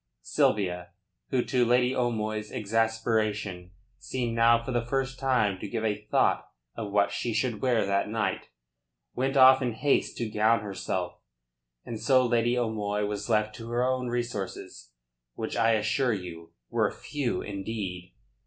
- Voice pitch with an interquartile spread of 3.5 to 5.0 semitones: No, average, 2.9 semitones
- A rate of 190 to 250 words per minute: No, average, 155 wpm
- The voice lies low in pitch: Yes, low, 110 Hz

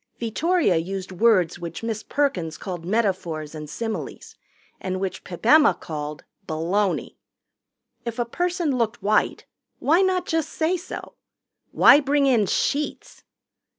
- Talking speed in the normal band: No, slow, 130 wpm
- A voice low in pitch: No, high, 215 Hz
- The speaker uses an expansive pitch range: Yes, wide, 8.4 semitones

